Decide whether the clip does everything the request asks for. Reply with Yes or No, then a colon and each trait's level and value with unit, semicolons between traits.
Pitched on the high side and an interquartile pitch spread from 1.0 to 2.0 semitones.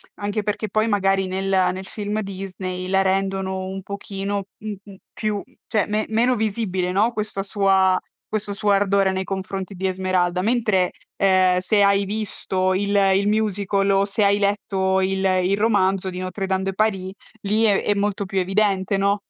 Yes: high, 195 Hz; narrow, 1.5 semitones